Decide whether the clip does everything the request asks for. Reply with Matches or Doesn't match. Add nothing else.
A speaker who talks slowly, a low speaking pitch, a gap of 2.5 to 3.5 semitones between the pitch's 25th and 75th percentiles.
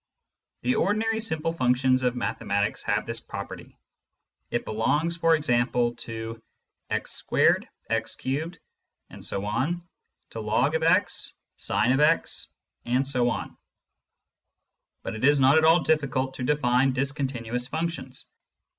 Doesn't match